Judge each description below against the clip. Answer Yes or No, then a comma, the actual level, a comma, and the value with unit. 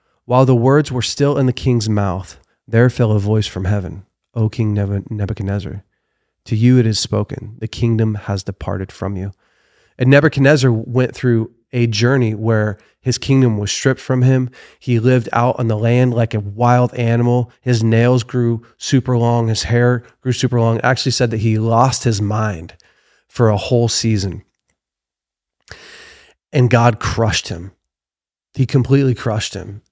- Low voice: Yes, low, 115 Hz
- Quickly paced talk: No, average, 165 wpm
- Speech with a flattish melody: No, average, 3.2 semitones